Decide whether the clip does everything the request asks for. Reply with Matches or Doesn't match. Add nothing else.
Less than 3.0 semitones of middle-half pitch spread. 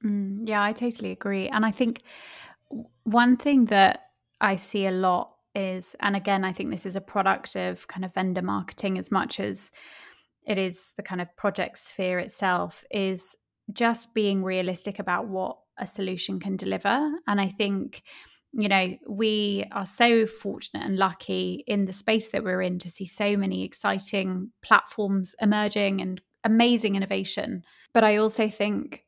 Matches